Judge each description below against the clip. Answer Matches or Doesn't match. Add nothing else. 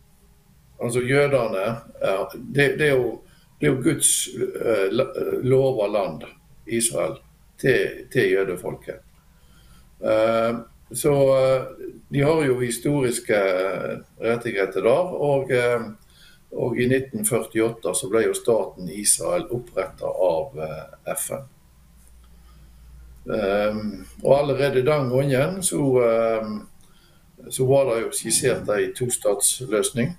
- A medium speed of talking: Doesn't match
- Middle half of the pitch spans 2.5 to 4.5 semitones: Matches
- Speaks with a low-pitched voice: Matches